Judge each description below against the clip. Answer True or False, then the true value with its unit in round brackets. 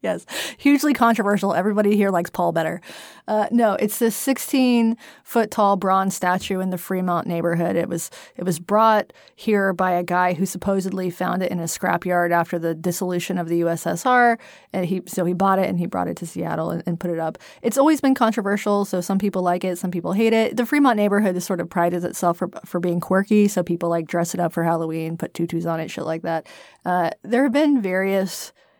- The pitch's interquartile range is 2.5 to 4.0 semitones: True (3.5 semitones)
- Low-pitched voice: False (185 Hz)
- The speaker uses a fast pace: True (215 wpm)